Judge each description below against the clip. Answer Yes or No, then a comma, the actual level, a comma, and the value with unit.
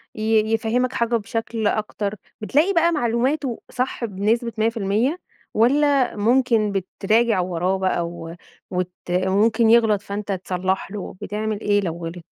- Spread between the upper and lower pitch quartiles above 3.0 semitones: Yes, average, 3.6 semitones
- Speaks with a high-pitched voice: Yes, high, 215 Hz